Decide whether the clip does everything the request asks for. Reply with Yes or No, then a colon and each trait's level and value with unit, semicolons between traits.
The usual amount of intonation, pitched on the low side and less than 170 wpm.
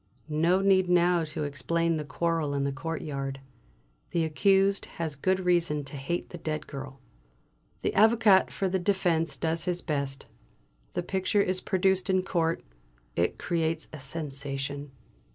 No: average, 4.3 semitones; medium, 165 Hz; average, 150 wpm